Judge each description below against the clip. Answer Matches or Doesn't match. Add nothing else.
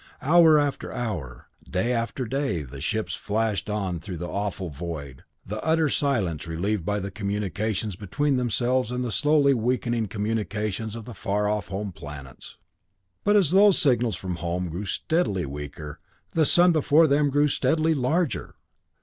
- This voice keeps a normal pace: Matches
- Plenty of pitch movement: Matches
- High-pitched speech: Doesn't match